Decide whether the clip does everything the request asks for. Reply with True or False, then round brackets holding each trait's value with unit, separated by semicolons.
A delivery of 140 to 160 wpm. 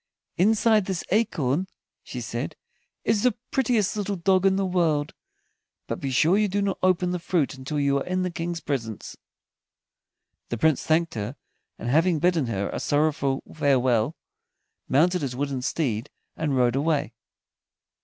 True (155 wpm)